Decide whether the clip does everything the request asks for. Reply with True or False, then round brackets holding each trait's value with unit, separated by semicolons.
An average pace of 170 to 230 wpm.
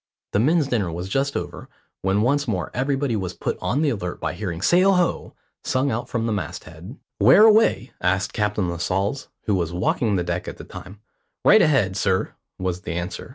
True (200 wpm)